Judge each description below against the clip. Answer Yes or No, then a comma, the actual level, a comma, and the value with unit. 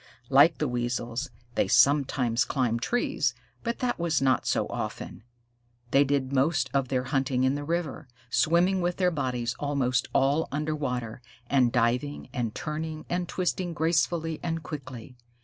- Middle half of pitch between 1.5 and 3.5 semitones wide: No, average, 4.2 semitones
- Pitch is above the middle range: No, medium, 140 Hz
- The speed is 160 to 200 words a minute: No, average, 150 wpm